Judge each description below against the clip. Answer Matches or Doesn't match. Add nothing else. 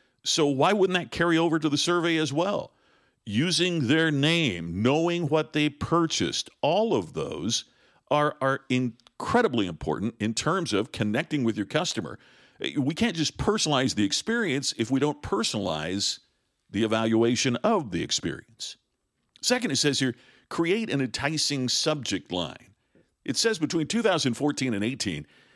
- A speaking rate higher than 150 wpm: Doesn't match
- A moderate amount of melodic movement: Doesn't match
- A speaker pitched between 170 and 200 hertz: Doesn't match